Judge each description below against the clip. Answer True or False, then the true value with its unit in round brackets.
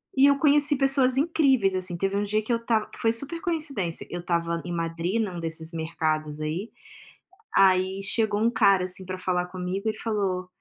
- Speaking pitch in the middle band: False (195 Hz)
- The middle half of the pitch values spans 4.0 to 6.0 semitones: True (4.8 semitones)